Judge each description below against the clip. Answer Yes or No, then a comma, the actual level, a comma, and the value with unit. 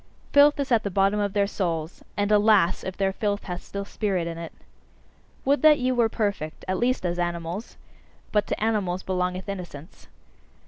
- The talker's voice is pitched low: No, high, 200 Hz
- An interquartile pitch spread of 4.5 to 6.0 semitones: No, average, 3.3 semitones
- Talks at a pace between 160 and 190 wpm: Yes, average, 180 wpm